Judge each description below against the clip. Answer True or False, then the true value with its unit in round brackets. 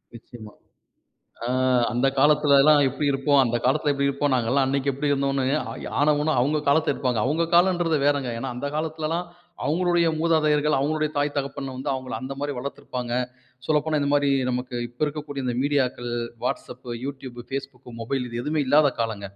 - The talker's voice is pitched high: False (140 Hz)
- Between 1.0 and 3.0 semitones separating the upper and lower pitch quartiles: True (2.7 semitones)